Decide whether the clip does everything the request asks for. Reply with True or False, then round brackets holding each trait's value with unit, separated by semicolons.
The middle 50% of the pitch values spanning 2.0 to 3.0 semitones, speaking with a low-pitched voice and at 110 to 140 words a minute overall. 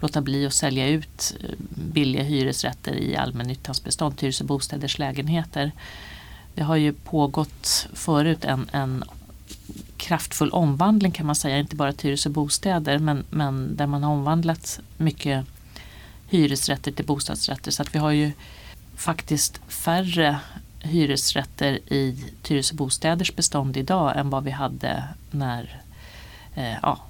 False (2.5 semitones; 145 Hz; 135 wpm)